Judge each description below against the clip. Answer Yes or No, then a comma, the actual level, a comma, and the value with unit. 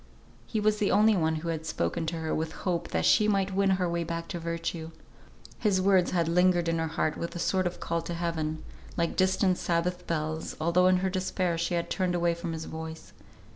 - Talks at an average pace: No, fast, 225 wpm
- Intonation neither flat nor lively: No, narrow, 2.1 semitones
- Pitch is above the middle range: No, medium, 170 Hz